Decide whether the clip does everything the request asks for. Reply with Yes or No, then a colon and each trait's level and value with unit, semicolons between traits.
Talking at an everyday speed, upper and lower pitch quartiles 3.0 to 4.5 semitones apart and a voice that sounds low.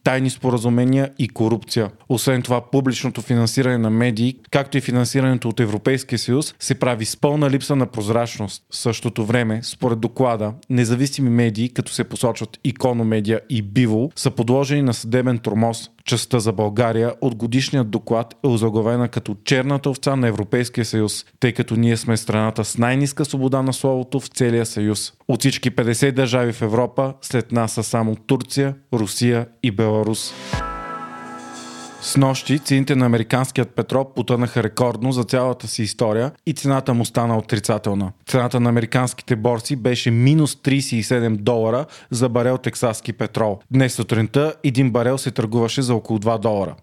No: average, 155 wpm; narrow, 2.6 semitones; low, 120 Hz